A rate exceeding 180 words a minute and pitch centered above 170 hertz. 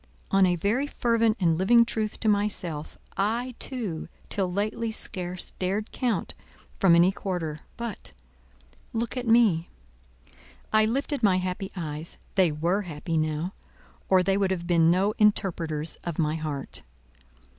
No: average, 140 wpm; medium, 185 Hz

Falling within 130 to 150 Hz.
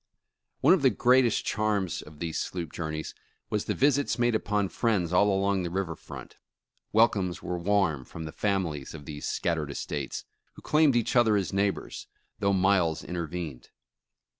No: very low, 95 Hz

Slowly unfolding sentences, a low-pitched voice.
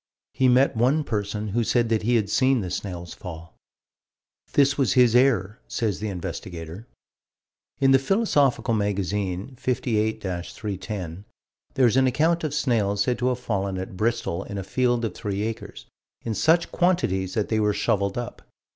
No: average, 165 wpm; low, 110 Hz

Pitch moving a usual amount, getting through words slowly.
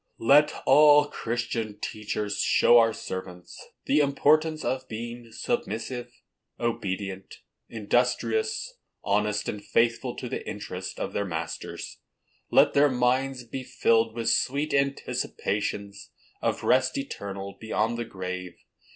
Yes: average, 4.6 semitones; slow, 115 wpm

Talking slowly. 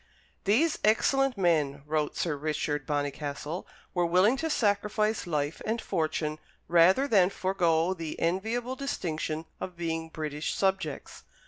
Yes: slow, 125 wpm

